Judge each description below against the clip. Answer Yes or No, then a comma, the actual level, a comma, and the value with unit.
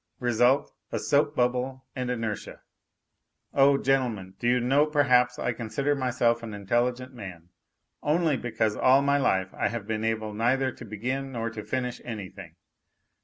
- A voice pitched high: No, low, 125 Hz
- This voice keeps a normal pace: Yes, average, 155 wpm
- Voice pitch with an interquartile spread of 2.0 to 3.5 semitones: Yes, average, 3.2 semitones